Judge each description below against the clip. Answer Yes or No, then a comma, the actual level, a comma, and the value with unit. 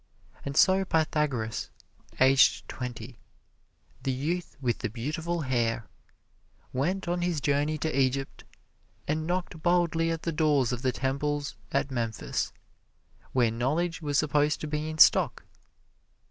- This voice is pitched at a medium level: Yes, medium, 145 Hz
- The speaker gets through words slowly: Yes, slow, 130 wpm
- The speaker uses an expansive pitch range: No, average, 3.9 semitones